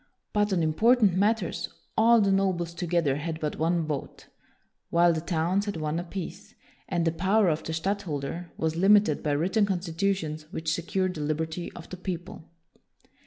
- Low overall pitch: No, medium, 175 Hz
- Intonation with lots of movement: No, average, 3.3 semitones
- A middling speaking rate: Yes, average, 165 wpm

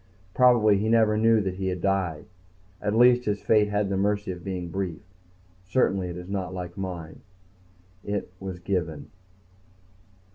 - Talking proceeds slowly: No, average, 155 wpm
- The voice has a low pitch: Yes, very low, 95 Hz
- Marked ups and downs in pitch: No, average, 2.7 semitones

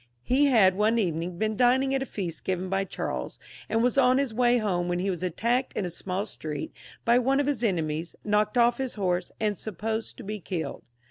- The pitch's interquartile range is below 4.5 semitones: No, average, 5.0 semitones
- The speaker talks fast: Yes, fast, 215 wpm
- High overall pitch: Yes, high, 210 Hz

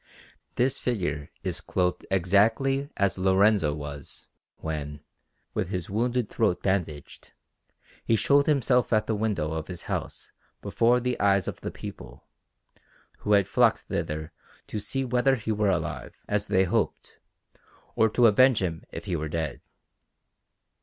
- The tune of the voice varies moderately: No, wide, 5.8 semitones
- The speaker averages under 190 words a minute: Yes, average, 145 wpm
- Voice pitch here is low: Yes, low, 100 Hz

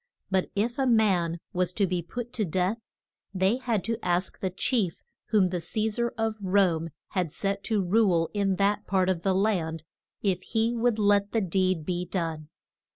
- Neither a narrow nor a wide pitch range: Yes, average, 3.5 semitones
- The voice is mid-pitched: No, high, 195 Hz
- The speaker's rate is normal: Yes, average, 185 wpm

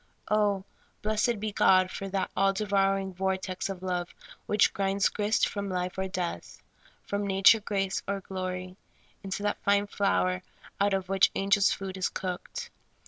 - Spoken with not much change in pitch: Yes, narrow, 1.3 semitones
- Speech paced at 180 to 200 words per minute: No, average, 160 wpm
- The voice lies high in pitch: Yes, high, 195 Hz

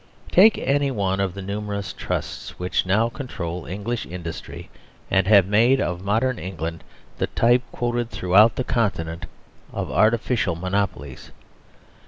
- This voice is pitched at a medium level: No, low, 100 Hz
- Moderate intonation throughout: Yes, average, 4.5 semitones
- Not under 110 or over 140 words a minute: Yes, slow, 135 wpm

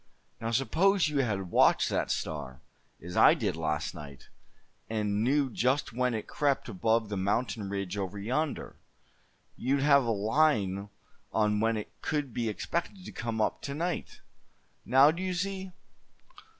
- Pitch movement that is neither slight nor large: No, wide, 6.0 semitones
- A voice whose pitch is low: Yes, low, 115 Hz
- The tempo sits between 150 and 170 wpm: Yes, average, 155 wpm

